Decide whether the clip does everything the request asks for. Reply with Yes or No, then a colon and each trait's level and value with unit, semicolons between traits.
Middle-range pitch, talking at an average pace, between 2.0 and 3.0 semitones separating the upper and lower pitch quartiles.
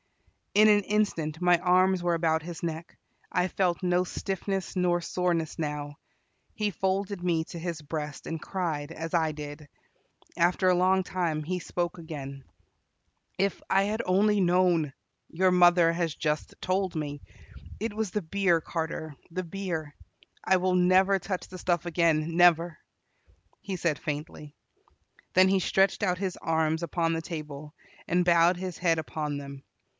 Yes: medium, 175 Hz; average, 155 wpm; narrow, 2.6 semitones